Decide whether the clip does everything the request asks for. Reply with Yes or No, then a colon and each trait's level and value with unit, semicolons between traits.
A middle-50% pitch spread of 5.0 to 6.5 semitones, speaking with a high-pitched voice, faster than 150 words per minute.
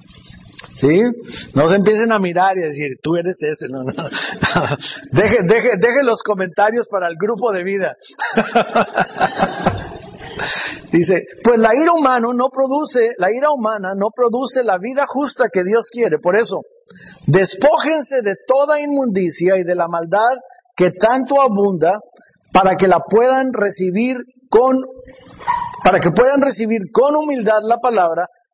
No: wide, 5.6 semitones; high, 225 Hz; average, 145 wpm